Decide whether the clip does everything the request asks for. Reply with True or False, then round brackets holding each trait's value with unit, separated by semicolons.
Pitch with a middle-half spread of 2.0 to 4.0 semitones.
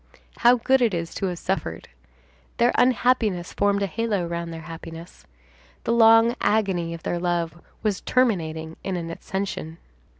False (5.2 semitones)